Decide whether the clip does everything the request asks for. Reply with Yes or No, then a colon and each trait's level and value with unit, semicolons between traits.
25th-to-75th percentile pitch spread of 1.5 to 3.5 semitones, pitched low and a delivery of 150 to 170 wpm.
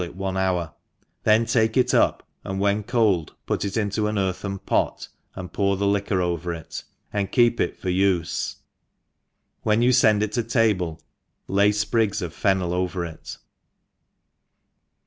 Yes: average, 2.8 semitones; low, 100 Hz; average, 155 wpm